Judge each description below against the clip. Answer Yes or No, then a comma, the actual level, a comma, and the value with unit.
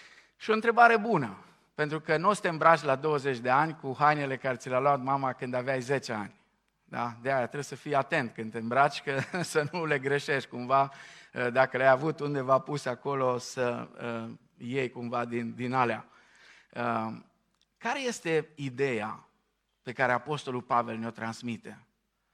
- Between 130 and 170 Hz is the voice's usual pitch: Yes, low, 135 Hz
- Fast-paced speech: Yes, fast, 175 wpm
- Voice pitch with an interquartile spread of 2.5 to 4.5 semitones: Yes, average, 3.4 semitones